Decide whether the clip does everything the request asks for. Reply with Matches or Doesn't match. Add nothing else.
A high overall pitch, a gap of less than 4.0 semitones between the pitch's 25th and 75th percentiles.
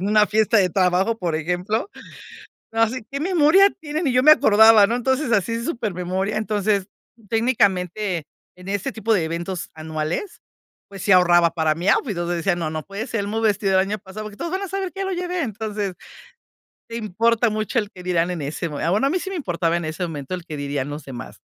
Doesn't match